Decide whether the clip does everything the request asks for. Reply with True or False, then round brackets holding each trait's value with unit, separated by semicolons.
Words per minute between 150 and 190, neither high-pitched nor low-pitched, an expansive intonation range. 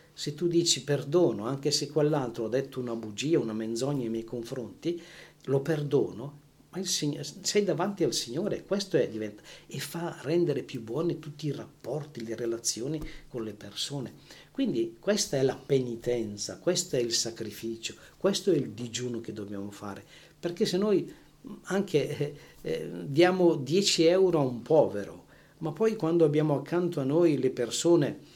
True (165 wpm; 145 Hz; 6.1 semitones)